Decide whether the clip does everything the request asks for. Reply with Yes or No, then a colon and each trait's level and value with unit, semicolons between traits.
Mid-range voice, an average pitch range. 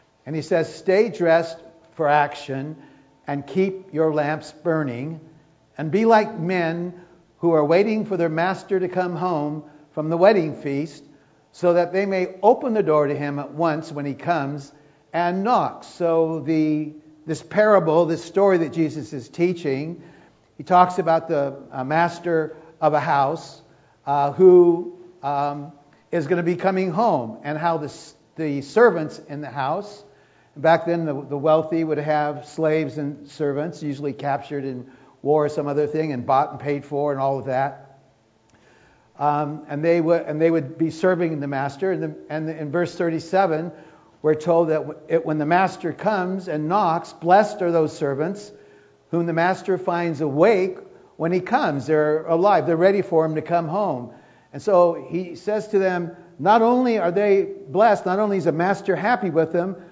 Yes: medium, 160 Hz; average, 3.1 semitones